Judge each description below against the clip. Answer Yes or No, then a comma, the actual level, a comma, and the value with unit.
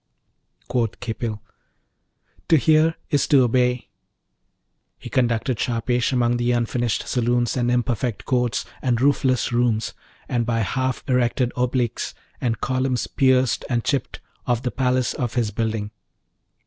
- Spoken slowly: Yes, slow, 130 wpm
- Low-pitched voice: Yes, low, 125 Hz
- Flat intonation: Yes, narrow, 1.5 semitones